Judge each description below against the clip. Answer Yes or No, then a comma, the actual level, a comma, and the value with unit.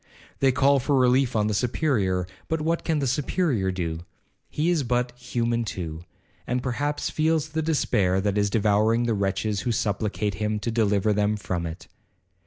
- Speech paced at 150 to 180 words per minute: Yes, average, 175 wpm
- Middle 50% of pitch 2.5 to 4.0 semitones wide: No, average, 5.2 semitones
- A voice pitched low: Yes, low, 115 Hz